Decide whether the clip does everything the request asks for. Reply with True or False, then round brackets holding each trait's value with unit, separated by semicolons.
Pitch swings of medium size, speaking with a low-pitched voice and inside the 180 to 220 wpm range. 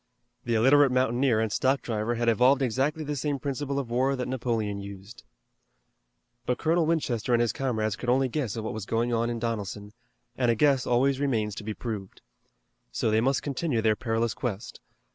True (3.4 semitones; 120 Hz; 190 wpm)